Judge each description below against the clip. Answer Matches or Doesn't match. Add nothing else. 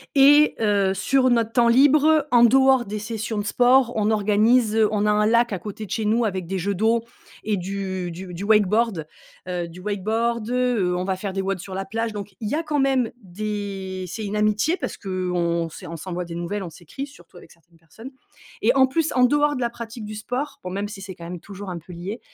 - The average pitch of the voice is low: Doesn't match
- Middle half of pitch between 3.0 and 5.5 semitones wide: Matches